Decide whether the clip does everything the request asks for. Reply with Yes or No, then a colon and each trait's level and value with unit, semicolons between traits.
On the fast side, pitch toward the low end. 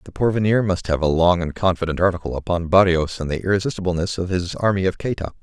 Yes: fast, 210 wpm; very low, 90 Hz